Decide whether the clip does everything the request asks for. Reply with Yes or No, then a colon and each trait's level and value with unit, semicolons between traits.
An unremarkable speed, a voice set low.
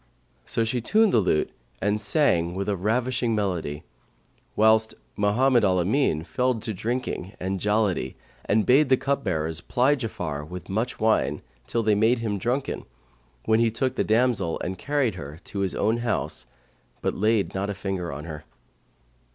Yes: average, 165 wpm; low, 105 Hz